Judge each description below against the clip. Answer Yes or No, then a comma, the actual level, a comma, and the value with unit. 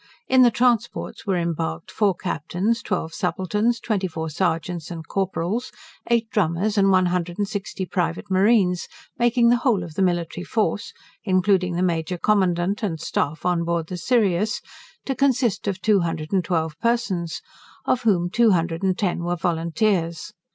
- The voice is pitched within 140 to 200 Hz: Yes, medium, 185 Hz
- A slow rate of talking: No, average, 165 wpm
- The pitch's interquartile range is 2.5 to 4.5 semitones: Yes, average, 3.8 semitones